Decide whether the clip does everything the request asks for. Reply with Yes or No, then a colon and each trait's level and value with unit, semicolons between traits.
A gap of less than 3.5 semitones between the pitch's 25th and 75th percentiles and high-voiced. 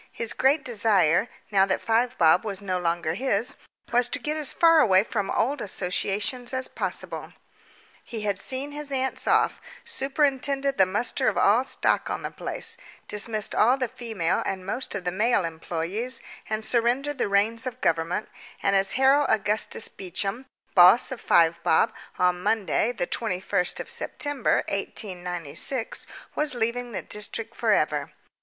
No: average, 5.3 semitones; high, 220 Hz